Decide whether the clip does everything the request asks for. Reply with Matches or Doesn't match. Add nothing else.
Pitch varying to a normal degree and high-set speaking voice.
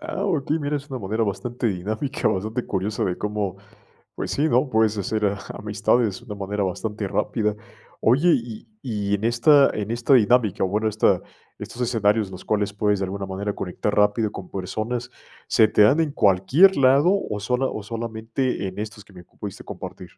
Doesn't match